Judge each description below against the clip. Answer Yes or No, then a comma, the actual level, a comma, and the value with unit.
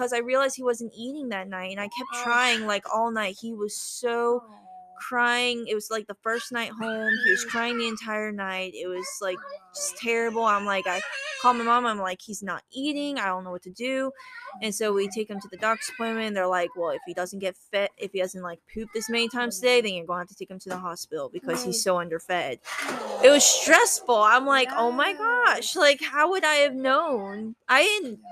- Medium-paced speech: No, fast, 235 wpm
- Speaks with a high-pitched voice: Yes, high, 225 Hz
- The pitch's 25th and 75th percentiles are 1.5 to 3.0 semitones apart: No, average, 4.2 semitones